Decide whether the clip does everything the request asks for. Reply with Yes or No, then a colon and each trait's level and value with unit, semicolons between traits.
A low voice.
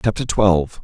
Yes: low, 100 Hz